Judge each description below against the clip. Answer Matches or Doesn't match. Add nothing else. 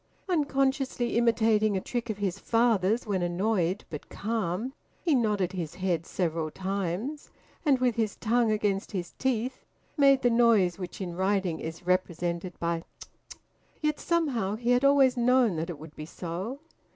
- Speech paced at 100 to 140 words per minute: Doesn't match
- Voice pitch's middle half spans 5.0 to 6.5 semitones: Matches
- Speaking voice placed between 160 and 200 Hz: Doesn't match